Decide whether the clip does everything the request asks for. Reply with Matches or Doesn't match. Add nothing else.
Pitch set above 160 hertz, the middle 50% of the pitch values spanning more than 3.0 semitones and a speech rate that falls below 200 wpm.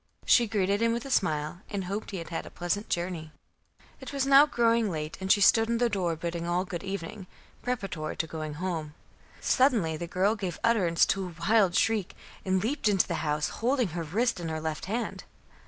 Doesn't match